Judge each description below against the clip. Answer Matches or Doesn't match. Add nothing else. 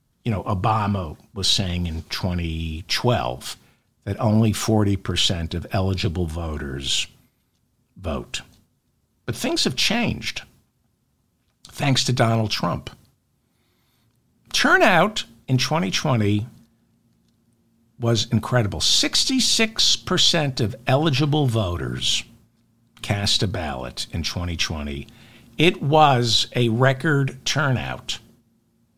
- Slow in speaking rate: Matches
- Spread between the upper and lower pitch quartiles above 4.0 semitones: Matches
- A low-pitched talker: Matches